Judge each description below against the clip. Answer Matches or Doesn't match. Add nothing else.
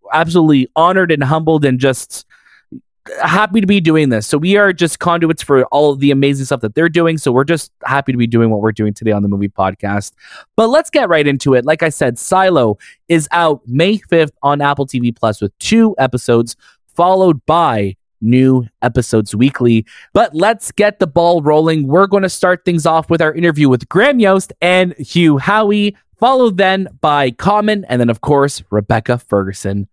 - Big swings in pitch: Matches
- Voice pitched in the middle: Matches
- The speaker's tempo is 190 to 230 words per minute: Matches